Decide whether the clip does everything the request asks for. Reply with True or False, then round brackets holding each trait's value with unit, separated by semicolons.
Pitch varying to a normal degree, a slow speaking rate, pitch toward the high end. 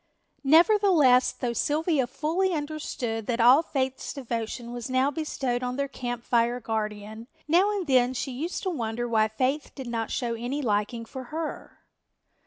False (4.2 semitones; 160 wpm; 255 Hz)